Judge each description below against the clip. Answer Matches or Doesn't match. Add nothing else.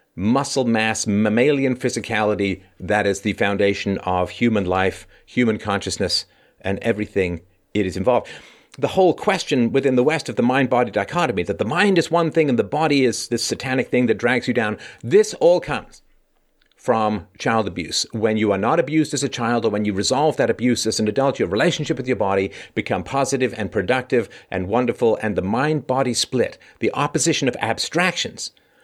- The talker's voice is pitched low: Matches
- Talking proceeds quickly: Doesn't match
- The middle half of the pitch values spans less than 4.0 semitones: Doesn't match